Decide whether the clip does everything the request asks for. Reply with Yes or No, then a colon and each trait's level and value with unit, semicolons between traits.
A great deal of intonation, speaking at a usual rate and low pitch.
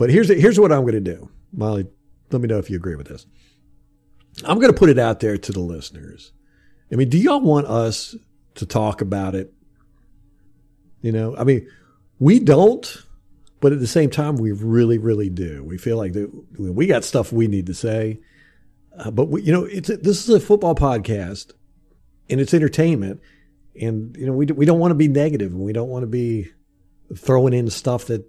No: wide, 6.2 semitones; fast, 210 wpm; low, 115 Hz